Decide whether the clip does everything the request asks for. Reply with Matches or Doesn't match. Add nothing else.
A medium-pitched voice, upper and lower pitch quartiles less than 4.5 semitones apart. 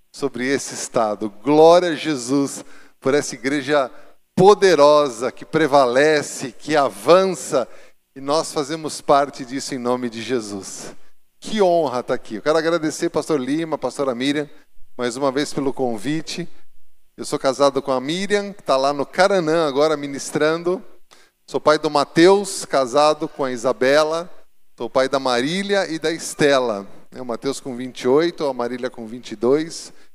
Matches